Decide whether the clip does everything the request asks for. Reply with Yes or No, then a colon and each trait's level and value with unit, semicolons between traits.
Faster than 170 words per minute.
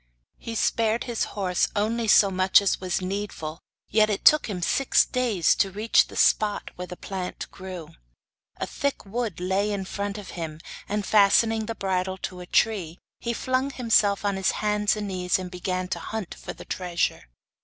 Yes: average, 185 wpm